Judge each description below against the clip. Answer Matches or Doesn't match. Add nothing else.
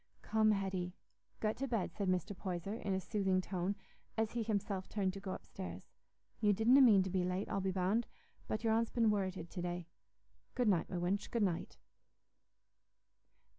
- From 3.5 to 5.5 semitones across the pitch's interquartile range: Doesn't match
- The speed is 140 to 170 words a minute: Doesn't match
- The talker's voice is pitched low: Doesn't match